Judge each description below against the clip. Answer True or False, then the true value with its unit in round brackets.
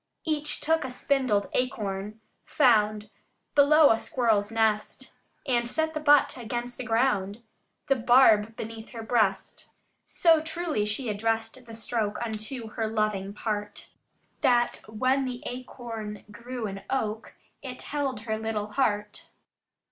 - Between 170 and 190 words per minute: False (135 wpm)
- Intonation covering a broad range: False (3.5 semitones)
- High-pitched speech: True (230 Hz)